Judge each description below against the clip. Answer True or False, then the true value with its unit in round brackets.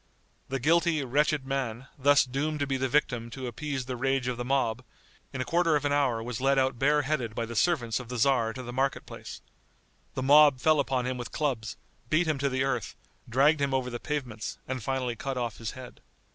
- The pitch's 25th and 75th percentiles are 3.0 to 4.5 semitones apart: False (2.6 semitones)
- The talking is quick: True (220 wpm)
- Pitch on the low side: True (130 Hz)